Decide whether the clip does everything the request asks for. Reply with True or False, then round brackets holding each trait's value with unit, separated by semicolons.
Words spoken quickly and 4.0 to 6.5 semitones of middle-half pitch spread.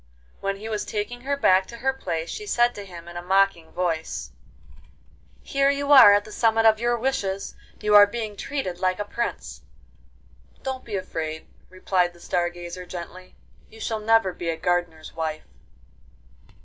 False (175 wpm; 4.6 semitones)